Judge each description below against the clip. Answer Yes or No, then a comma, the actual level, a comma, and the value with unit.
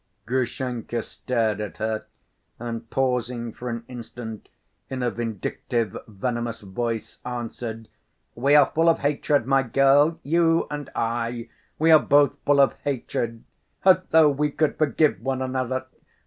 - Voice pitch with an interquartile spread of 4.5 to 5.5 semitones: No, average, 3.5 semitones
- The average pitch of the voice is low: Yes, low, 125 Hz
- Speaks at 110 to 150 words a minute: Yes, average, 140 wpm